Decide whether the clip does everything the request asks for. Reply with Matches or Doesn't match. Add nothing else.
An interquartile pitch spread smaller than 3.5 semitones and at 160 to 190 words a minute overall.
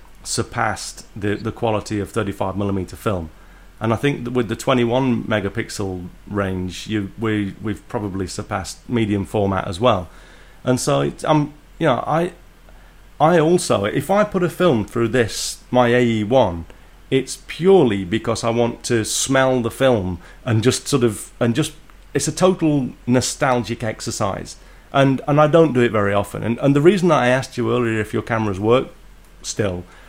Doesn't match